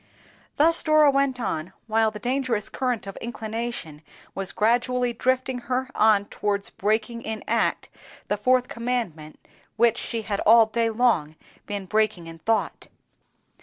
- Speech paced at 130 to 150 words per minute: Yes, average, 140 wpm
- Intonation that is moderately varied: Yes, average, 3.2 semitones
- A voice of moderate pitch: No, high, 225 Hz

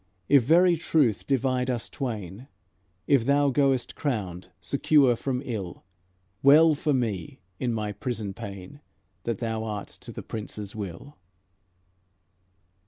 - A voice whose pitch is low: Yes, low, 120 Hz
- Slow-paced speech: Yes, slow, 125 wpm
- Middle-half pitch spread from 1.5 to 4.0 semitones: No, average, 5.0 semitones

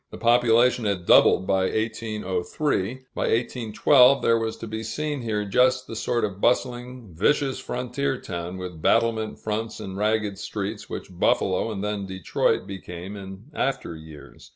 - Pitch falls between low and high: No, low, 110 Hz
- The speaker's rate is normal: Yes, average, 155 wpm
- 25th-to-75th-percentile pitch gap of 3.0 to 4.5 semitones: Yes, average, 4.1 semitones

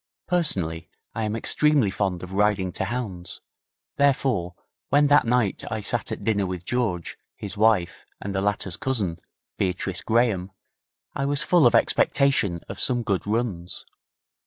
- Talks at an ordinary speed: Yes, average, 150 wpm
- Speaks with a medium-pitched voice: No, low, 105 Hz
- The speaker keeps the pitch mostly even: No, average, 5.2 semitones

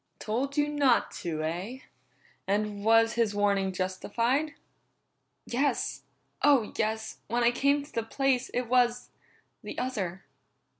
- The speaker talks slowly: Yes, slow, 130 wpm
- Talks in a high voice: Yes, high, 230 Hz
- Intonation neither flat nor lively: Yes, average, 4.3 semitones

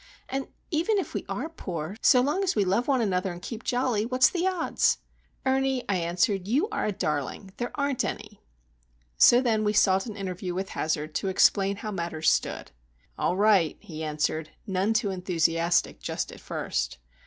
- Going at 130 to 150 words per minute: No, average, 180 wpm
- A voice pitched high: Yes, high, 200 Hz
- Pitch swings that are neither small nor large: No, wide, 6.1 semitones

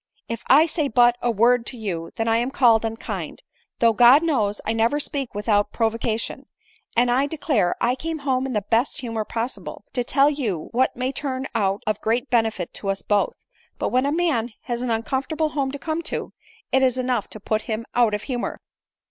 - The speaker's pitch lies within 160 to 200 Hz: No, high, 240 Hz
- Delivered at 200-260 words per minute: Yes, fast, 205 wpm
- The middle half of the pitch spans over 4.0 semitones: No, average, 3.3 semitones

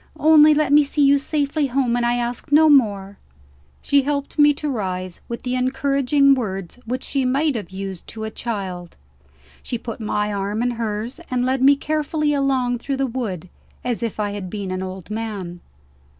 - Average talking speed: Yes, average, 190 wpm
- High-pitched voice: Yes, high, 245 Hz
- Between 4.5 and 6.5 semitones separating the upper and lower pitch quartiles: Yes, average, 5.1 semitones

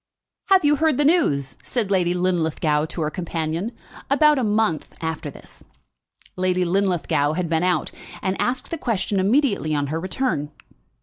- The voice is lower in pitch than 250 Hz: Yes, medium, 185 Hz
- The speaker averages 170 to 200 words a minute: No, average, 160 wpm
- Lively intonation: Yes, wide, 7.0 semitones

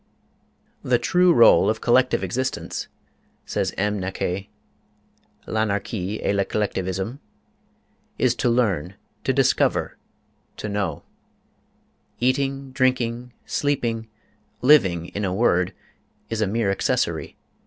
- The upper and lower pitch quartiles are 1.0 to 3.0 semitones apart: No, average, 4.5 semitones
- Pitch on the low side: Yes, low, 110 Hz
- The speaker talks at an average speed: No, slow, 90 wpm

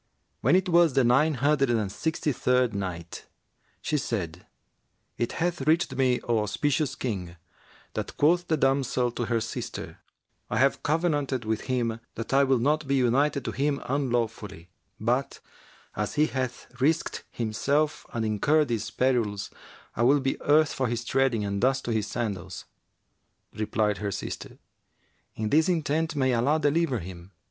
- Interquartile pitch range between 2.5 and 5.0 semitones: Yes, average, 4.6 semitones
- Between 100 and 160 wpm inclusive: Yes, average, 155 wpm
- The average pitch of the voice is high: No, low, 130 Hz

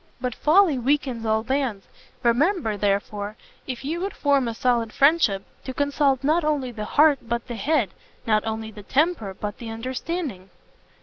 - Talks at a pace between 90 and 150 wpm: No, average, 165 wpm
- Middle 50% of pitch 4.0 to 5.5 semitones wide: Yes, average, 4.9 semitones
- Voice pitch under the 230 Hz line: No, very high, 250 Hz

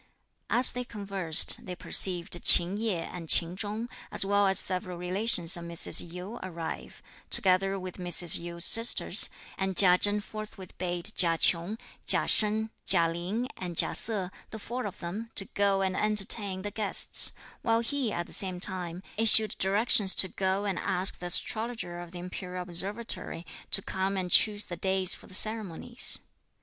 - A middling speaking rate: Yes, average, 170 wpm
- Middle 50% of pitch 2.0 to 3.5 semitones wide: Yes, average, 3.0 semitones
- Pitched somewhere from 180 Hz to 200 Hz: Yes, high, 190 Hz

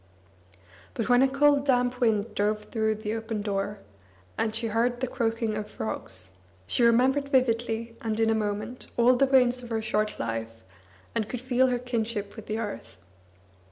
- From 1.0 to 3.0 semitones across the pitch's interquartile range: Yes, narrow, 2.6 semitones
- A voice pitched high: Yes, high, 225 Hz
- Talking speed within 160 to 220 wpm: Yes, average, 175 wpm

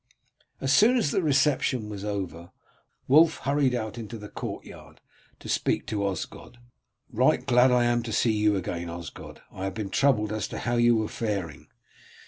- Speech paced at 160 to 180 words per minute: Yes, average, 175 wpm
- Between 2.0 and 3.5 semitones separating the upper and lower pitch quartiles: No, average, 4.3 semitones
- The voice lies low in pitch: Yes, low, 110 Hz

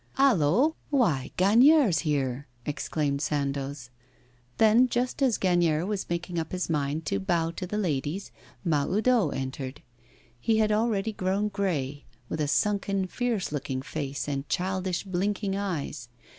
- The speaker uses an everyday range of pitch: No, wide, 6.3 semitones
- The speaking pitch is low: No, medium, 175 Hz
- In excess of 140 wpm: No, slow, 135 wpm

